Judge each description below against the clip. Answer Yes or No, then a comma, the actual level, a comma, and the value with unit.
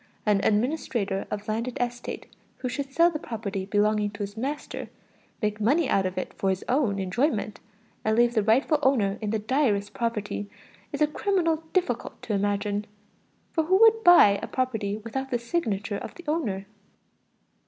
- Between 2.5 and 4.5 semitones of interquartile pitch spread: No, average, 5.2 semitones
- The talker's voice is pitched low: No, high, 225 Hz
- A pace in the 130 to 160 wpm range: No, average, 170 wpm